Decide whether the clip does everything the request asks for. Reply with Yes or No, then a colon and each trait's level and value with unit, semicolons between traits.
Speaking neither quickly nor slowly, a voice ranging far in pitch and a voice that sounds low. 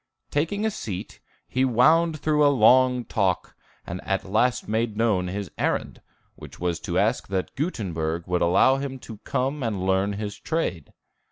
Yes: average, 165 wpm; wide, 6.1 semitones; low, 110 Hz